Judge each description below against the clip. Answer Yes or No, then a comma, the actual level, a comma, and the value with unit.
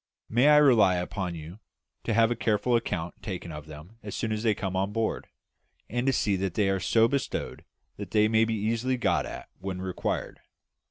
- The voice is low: Yes, low, 105 Hz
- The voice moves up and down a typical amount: Yes, average, 3.7 semitones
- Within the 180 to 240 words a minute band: Yes, average, 195 wpm